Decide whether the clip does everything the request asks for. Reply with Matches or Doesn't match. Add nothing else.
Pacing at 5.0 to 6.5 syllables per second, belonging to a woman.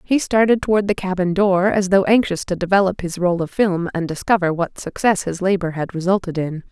Matches